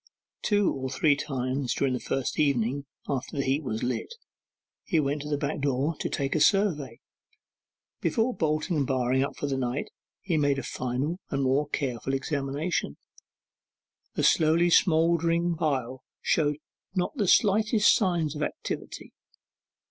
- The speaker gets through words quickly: No, average, 150 wpm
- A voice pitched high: No, medium, 145 Hz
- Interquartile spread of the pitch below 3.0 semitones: No, average, 3.7 semitones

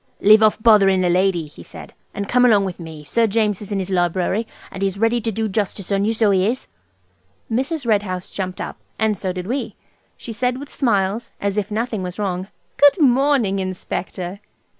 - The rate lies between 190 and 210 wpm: Yes, fast, 205 wpm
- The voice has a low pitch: No, high, 200 Hz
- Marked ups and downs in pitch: No, average, 3.3 semitones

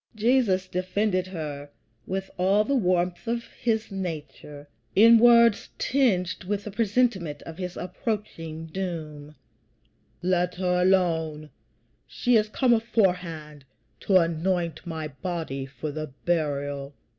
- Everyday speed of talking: No, slow, 120 wpm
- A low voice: No, medium, 180 Hz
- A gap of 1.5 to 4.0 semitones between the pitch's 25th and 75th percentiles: No, average, 4.7 semitones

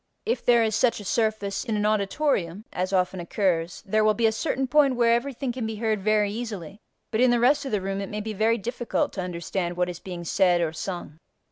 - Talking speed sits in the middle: No, fast, 235 wpm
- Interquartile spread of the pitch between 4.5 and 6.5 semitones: No, average, 4.0 semitones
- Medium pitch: No, high, 215 Hz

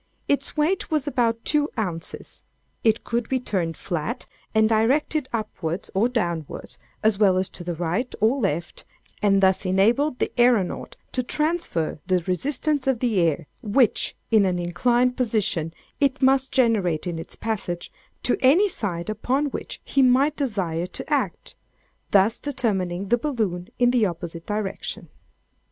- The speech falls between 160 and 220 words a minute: No, average, 150 wpm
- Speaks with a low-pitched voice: No, high, 220 Hz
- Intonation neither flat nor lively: No, wide, 6.1 semitones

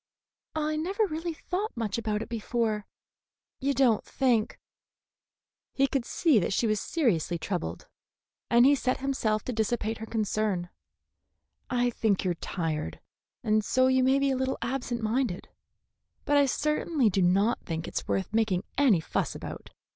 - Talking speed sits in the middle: Yes, average, 160 wpm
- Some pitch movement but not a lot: Yes, average, 4.5 semitones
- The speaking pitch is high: Yes, high, 235 Hz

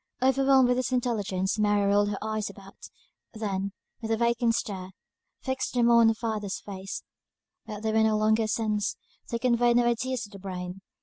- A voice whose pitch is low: No, high, 220 Hz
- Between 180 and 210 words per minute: Yes, average, 185 wpm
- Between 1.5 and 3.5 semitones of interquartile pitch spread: Yes, average, 2.7 semitones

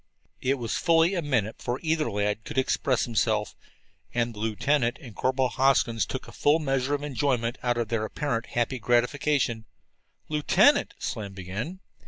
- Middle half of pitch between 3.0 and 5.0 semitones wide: Yes, average, 4.2 semitones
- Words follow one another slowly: No, average, 165 wpm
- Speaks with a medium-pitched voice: No, low, 125 Hz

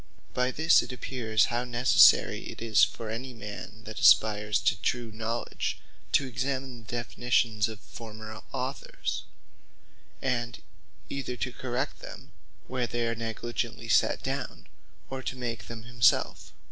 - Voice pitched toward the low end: Yes, low, 120 Hz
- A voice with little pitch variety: Yes, narrow, 2.3 semitones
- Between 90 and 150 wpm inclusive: Yes, average, 140 wpm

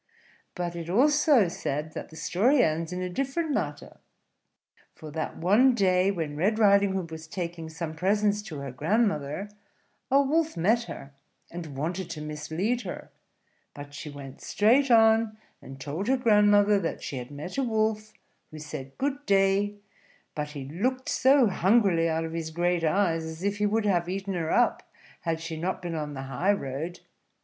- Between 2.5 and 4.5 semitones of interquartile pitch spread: No, average, 5.1 semitones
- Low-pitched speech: No, medium, 180 Hz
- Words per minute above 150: Yes, average, 180 wpm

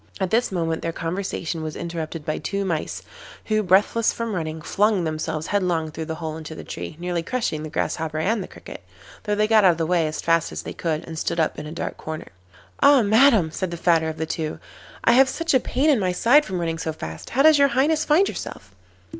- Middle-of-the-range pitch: Yes, medium, 175 Hz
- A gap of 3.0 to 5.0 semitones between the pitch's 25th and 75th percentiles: No, wide, 5.4 semitones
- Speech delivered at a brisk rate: Yes, fast, 235 wpm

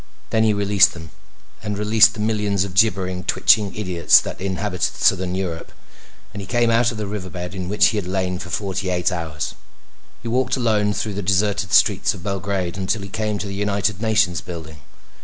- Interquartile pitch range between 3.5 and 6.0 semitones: No, narrow, 2.5 semitones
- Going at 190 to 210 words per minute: Yes, average, 195 wpm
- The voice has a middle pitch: No, low, 100 Hz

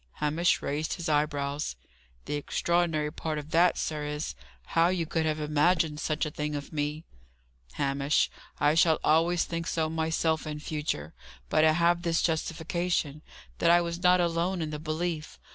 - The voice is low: No, medium, 160 Hz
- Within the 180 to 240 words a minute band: No, average, 165 wpm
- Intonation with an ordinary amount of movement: No, narrow, 2.1 semitones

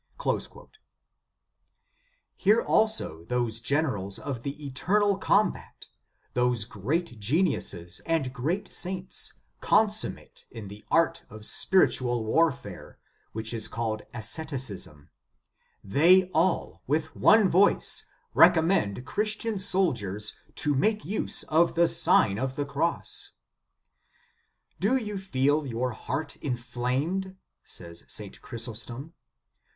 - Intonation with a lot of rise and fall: Yes, wide, 8.2 semitones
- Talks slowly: Yes, slow, 105 wpm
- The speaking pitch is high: No, medium, 140 Hz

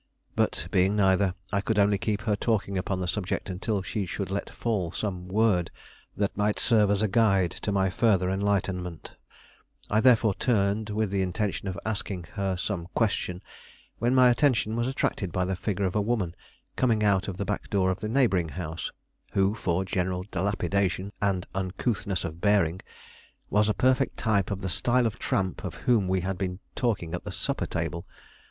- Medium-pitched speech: No, low, 100 Hz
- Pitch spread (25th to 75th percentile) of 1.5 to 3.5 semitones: Yes, narrow, 2.6 semitones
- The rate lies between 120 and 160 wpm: No, average, 185 wpm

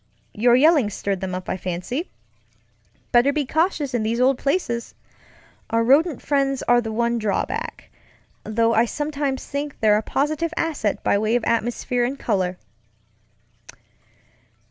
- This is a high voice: Yes, high, 240 Hz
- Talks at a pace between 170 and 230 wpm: No, average, 140 wpm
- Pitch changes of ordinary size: Yes, average, 4.4 semitones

